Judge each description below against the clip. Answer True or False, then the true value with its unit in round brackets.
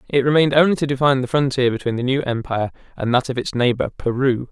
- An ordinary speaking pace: False (225 wpm)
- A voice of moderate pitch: False (130 Hz)